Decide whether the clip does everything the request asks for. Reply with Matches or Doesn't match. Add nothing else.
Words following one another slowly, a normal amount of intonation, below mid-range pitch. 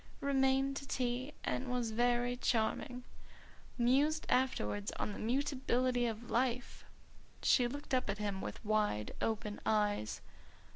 Doesn't match